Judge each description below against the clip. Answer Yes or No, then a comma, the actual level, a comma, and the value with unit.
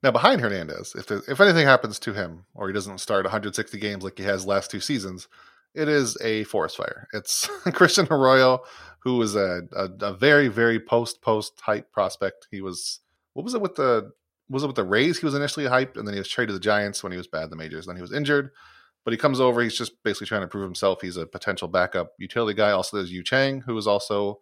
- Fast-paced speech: Yes, fast, 250 wpm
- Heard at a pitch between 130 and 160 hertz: No, low, 105 Hz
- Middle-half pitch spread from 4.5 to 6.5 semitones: Yes, average, 5.1 semitones